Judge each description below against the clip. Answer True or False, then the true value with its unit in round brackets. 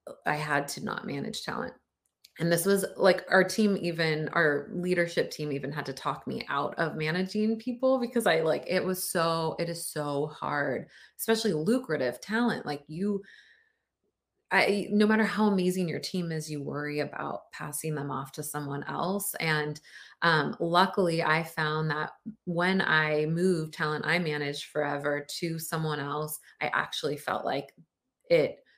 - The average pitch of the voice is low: False (165 Hz)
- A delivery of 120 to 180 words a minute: True (165 wpm)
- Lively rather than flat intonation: False (4.3 semitones)